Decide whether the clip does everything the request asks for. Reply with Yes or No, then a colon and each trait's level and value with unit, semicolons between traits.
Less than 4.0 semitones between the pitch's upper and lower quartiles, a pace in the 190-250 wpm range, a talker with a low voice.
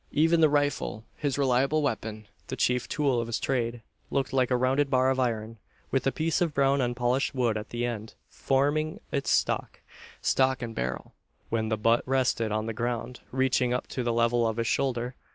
Yes: average, 2.8 semitones; average, 195 wpm; low, 125 Hz